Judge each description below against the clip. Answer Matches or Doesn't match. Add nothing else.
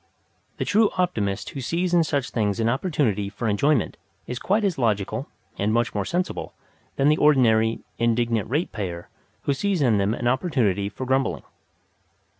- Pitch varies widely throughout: Matches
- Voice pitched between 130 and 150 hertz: Doesn't match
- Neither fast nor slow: Matches